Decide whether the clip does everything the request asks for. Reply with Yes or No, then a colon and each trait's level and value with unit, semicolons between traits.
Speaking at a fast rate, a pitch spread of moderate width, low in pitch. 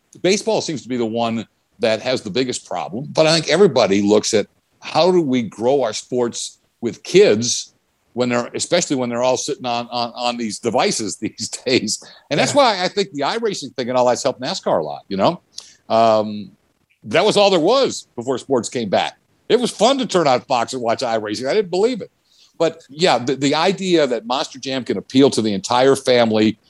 No: fast, 210 wpm; wide, 5.7 semitones; low, 125 Hz